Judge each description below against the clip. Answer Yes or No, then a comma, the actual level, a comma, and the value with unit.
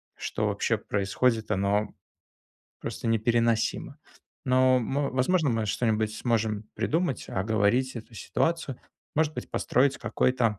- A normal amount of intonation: Yes, average, 3.2 semitones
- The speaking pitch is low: Yes, low, 115 Hz